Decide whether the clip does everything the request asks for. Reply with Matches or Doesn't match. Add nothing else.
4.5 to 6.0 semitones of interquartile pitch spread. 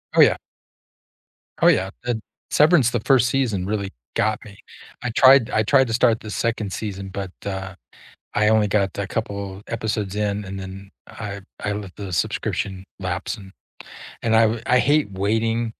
Doesn't match